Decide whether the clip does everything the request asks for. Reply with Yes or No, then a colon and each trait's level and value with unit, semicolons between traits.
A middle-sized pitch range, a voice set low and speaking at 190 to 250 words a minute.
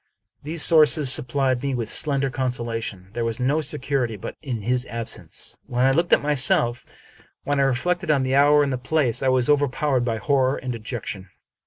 Yes: average, 3.1 semitones; low, 130 Hz; average, 195 wpm